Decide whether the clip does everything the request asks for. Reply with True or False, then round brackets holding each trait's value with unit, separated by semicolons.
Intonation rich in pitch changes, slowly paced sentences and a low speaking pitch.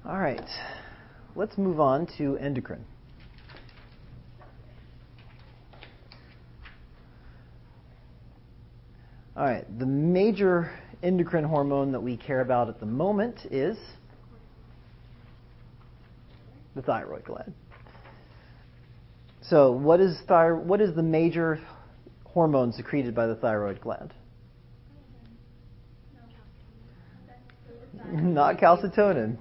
True (5.8 semitones; 80 wpm; 125 Hz)